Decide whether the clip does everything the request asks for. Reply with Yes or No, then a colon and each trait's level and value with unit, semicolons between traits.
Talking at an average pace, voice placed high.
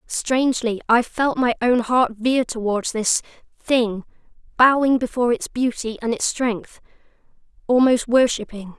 No: slow, 125 wpm; high, 240 Hz